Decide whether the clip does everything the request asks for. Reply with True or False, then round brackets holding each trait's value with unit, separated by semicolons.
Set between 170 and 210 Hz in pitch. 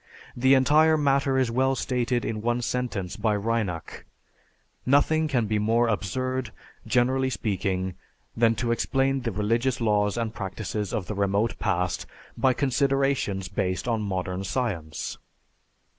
False (115 Hz)